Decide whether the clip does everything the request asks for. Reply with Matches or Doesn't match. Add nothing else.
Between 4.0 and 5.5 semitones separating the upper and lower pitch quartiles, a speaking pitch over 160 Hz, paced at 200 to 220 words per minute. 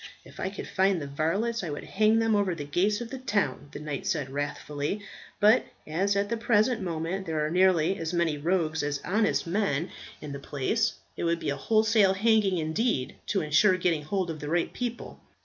Matches